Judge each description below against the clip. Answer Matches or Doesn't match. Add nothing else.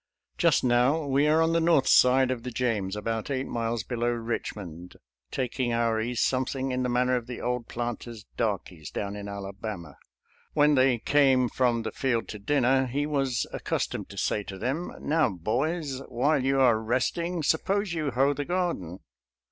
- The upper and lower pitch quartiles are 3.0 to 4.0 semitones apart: Matches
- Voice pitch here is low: Matches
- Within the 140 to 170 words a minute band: Doesn't match